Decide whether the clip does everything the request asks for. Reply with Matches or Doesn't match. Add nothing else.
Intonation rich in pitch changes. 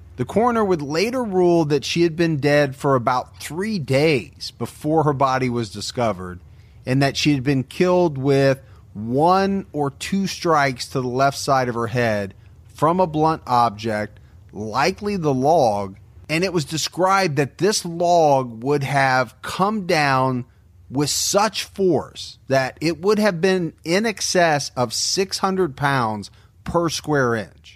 Matches